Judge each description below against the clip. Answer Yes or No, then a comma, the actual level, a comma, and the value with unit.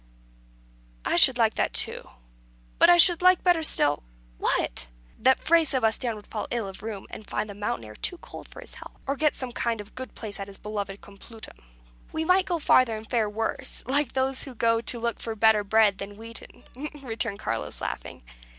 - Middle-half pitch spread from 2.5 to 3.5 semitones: No, average, 4.3 semitones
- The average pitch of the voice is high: Yes, high, 225 Hz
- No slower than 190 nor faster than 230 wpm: Yes, fast, 205 wpm